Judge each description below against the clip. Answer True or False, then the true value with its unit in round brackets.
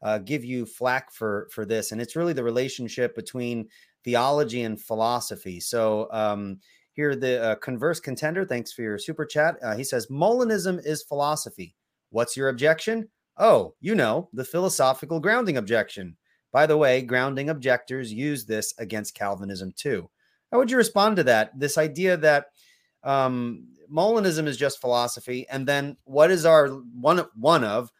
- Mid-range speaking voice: False (130 Hz)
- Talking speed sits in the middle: True (165 wpm)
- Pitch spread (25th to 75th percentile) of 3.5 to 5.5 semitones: True (5.0 semitones)